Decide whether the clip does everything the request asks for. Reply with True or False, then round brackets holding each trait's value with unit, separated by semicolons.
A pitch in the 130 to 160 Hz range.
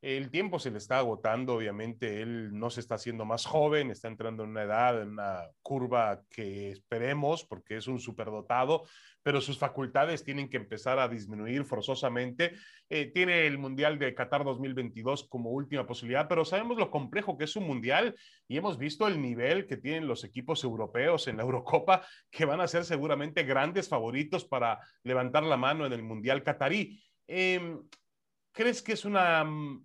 True (135 Hz)